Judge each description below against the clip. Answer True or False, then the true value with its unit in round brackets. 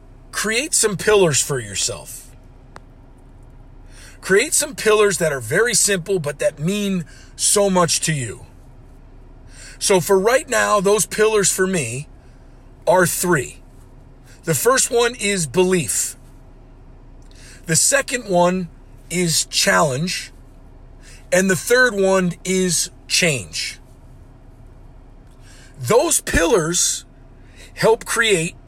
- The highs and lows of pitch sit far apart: True (7.5 semitones)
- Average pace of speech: False (105 wpm)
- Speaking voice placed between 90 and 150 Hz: False (165 Hz)